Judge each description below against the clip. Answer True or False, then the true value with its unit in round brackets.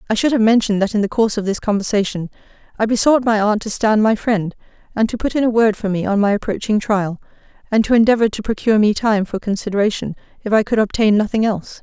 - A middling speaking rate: False (235 wpm)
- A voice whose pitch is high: True (215 Hz)